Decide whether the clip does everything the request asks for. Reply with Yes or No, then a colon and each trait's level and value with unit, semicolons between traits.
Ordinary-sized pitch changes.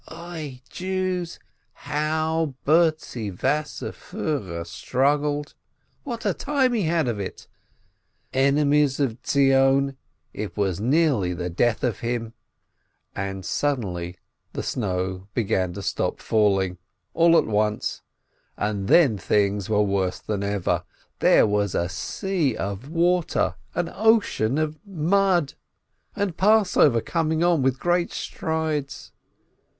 No: wide, 8.1 semitones